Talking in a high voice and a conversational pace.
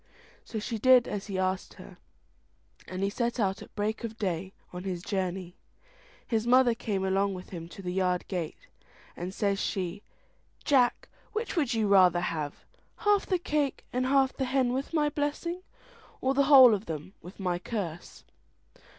Yes: high, 205 Hz; average, 175 wpm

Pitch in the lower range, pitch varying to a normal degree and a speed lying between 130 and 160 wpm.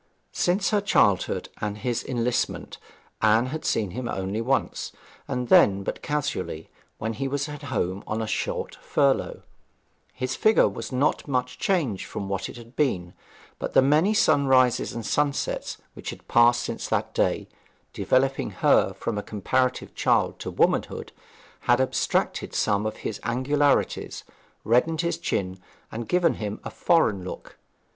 Yes: low, 125 Hz; average, 5.0 semitones; average, 150 wpm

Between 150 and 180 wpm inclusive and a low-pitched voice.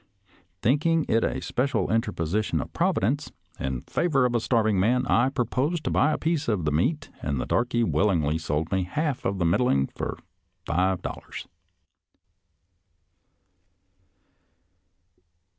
No: average, 140 wpm; low, 115 Hz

